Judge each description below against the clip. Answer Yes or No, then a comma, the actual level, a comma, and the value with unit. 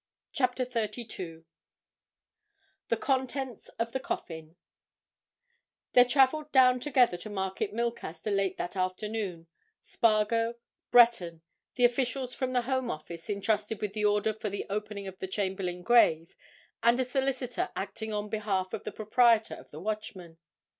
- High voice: Yes, high, 215 Hz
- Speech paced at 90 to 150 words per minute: Yes, average, 140 wpm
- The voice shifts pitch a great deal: No, average, 4.4 semitones